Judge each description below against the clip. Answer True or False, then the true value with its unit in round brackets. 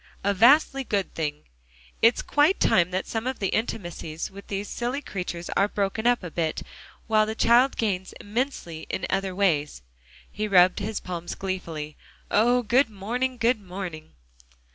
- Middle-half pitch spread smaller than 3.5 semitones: False (4.7 semitones)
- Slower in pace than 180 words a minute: True (160 wpm)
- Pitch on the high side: True (200 Hz)